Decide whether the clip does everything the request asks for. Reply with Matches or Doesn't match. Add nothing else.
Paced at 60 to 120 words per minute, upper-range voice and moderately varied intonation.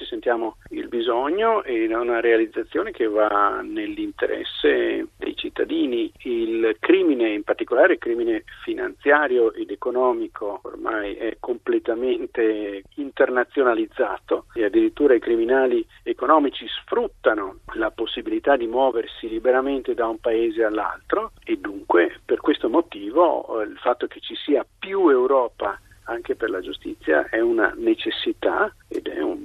Matches